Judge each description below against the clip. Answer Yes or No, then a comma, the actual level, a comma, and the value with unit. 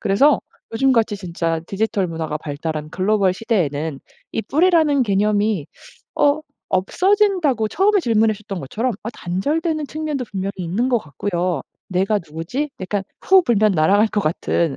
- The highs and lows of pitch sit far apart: Yes, wide, 7.2 semitones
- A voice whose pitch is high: Yes, high, 210 Hz